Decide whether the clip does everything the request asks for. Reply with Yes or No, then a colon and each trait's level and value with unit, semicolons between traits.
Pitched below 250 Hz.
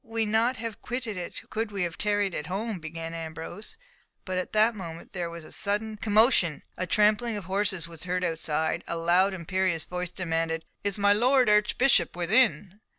Yes: high, 190 Hz